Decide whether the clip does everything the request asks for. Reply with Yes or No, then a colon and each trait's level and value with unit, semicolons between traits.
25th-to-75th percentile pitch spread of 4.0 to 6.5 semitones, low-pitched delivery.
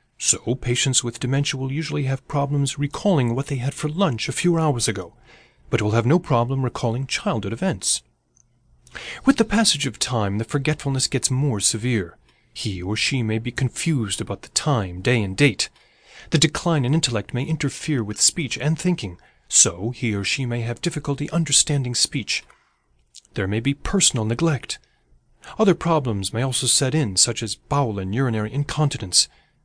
Yes: average, 4.5 semitones; low, 130 Hz